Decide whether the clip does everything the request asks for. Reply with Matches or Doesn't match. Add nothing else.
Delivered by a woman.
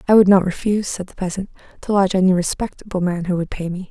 Matches